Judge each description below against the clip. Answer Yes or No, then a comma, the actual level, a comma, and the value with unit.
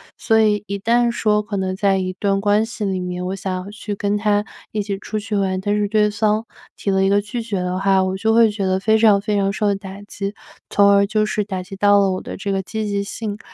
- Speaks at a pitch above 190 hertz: Yes, high, 205 Hz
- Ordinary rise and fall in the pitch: No, narrow, 1.5 semitones